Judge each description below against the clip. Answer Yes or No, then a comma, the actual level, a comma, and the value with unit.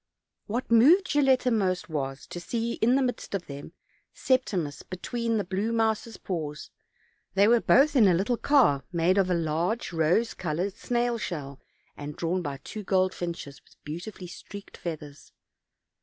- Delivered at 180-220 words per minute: No, average, 160 wpm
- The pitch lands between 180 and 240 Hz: Yes, high, 190 Hz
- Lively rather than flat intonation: Yes, wide, 5.9 semitones